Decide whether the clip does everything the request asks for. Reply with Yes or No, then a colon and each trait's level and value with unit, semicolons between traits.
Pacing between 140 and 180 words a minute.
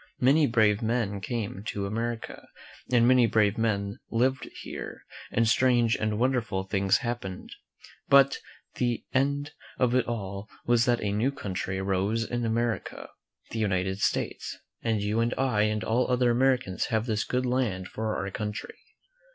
Yes: average, 160 wpm